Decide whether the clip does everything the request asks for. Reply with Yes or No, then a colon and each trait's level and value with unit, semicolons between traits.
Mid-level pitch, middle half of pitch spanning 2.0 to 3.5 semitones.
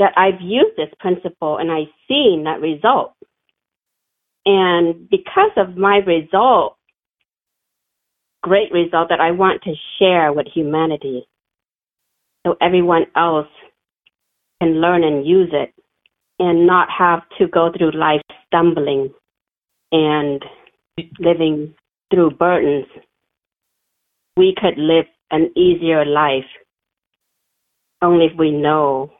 Yes: medium, 170 Hz; average, 2.9 semitones